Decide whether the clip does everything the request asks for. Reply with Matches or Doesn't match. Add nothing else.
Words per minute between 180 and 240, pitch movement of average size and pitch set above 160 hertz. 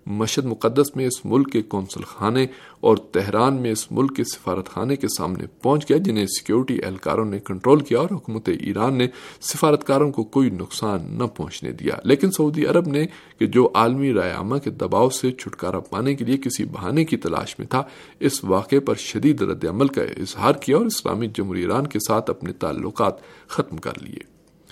Doesn't match